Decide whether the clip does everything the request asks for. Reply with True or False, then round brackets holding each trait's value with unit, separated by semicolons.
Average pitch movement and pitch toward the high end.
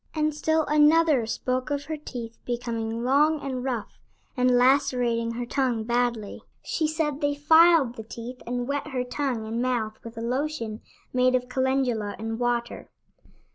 True (3.6 semitones; 250 Hz)